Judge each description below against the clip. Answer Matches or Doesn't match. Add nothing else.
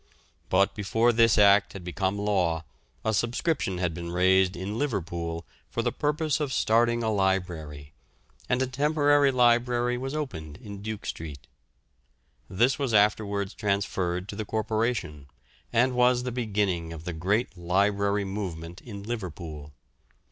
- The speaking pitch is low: Matches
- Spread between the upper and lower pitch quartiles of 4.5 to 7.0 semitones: Matches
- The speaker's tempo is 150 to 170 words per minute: Doesn't match